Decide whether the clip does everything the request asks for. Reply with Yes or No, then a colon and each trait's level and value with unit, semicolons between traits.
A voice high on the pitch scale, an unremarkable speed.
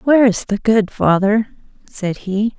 Yes: high, 210 Hz; average, 160 wpm